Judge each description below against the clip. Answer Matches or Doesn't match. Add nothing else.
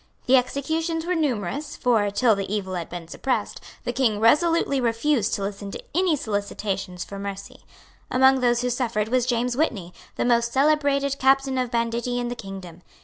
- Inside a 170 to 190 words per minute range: Matches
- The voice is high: Matches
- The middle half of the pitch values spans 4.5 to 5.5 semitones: Matches